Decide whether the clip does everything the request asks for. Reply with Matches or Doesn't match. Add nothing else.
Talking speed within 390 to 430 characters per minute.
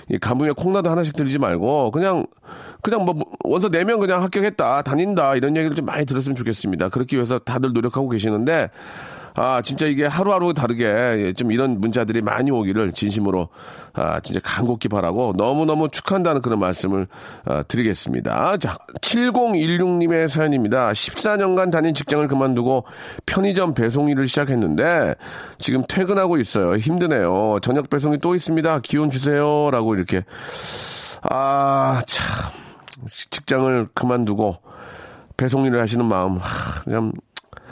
Doesn't match